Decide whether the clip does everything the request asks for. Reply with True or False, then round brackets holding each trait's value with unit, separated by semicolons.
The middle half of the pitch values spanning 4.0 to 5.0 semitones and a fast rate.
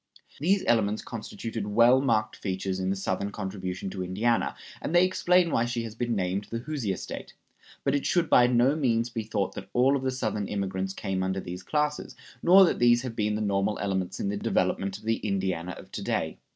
True (4.3 semitones; 210 wpm)